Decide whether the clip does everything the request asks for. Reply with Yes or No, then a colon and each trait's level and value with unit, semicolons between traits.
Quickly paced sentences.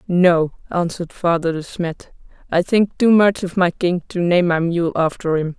No: average, 195 wpm